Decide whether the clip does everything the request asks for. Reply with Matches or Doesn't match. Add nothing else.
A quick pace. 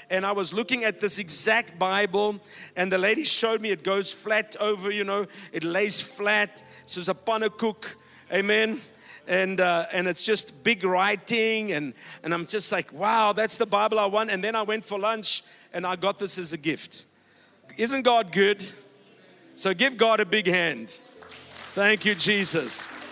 Doesn't match